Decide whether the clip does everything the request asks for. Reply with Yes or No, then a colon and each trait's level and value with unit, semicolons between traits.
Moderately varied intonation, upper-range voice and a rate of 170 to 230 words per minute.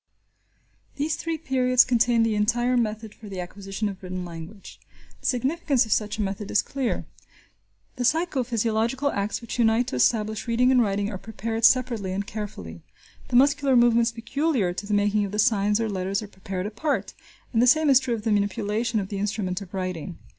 Yes: average, 3.7 semitones; high, 220 Hz; average, 190 wpm